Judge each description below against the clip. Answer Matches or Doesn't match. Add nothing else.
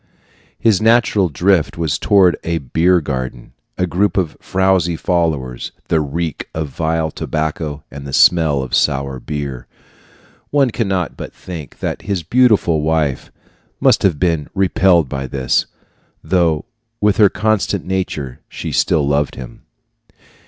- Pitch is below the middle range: Matches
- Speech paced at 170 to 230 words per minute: Doesn't match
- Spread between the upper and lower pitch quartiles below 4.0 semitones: Doesn't match